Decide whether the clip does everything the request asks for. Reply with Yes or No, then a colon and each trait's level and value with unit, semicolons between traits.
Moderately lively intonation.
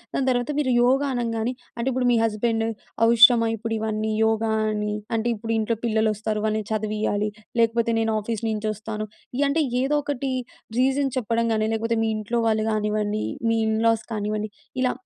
No: narrow, 1.8 semitones